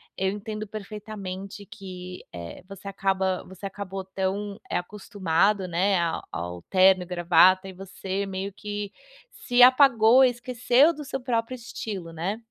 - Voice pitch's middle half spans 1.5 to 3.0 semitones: Yes, narrow, 2.5 semitones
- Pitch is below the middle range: No, high, 195 Hz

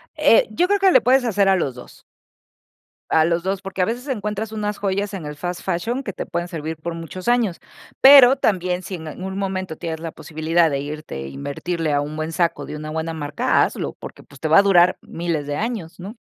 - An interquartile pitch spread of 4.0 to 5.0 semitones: Yes, average, 4.5 semitones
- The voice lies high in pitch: No, medium, 175 Hz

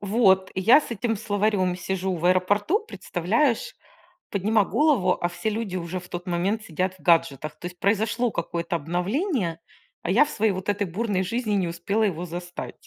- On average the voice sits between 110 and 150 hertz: No, high, 190 Hz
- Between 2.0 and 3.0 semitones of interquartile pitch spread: No, average, 3.8 semitones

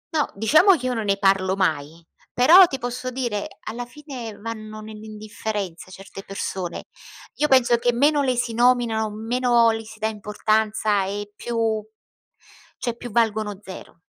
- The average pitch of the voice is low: No, high, 220 Hz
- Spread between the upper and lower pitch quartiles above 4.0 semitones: No, average, 2.9 semitones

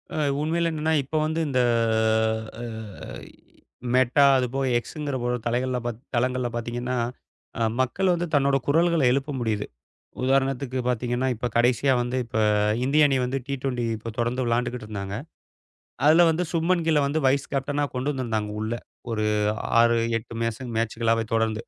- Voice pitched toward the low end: Yes, low, 130 Hz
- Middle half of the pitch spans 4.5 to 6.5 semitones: No, average, 3.4 semitones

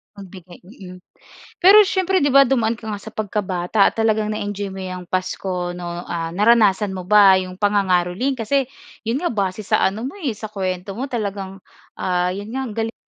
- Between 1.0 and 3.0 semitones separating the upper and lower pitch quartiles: No, average, 3.5 semitones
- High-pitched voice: Yes, high, 205 Hz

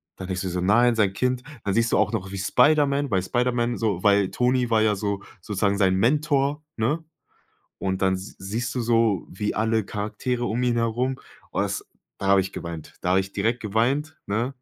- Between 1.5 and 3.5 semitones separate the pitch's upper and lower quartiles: No, average, 4.1 semitones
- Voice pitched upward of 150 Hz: No, low, 110 Hz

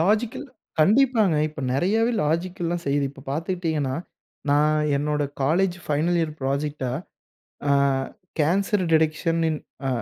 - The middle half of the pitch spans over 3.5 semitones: Yes, average, 3.9 semitones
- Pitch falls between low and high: Yes, medium, 160 Hz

